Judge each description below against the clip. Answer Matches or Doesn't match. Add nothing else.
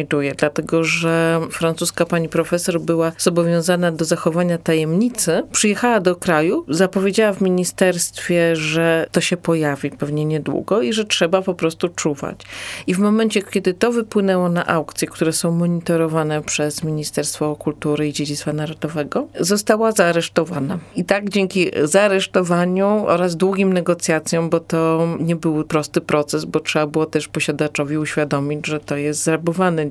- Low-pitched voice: Doesn't match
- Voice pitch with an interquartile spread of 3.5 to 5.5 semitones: Doesn't match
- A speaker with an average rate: Matches